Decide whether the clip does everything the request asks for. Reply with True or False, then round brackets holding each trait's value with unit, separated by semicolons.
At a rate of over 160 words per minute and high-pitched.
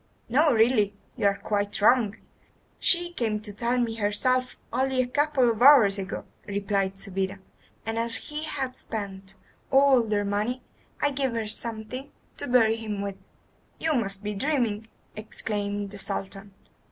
False (155 wpm; 220 Hz)